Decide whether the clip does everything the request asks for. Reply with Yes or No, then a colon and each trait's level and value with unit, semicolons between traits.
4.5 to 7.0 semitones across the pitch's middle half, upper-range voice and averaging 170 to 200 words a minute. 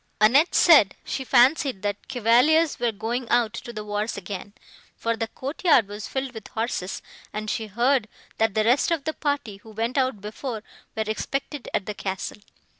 No: average, 4.1 semitones; high, 230 Hz; average, 180 wpm